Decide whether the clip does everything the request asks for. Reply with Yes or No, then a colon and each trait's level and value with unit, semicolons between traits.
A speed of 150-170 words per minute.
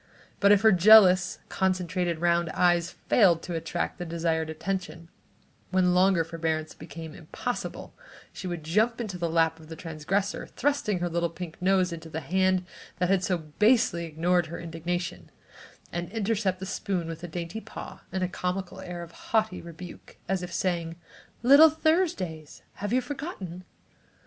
Yes: average, 160 wpm